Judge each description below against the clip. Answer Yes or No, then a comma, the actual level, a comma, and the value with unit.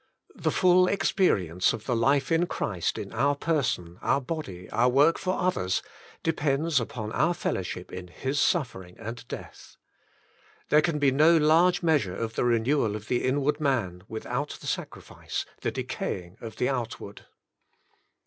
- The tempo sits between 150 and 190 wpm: Yes, average, 160 wpm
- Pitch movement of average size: No, wide, 6.4 semitones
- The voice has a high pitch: No, low, 130 Hz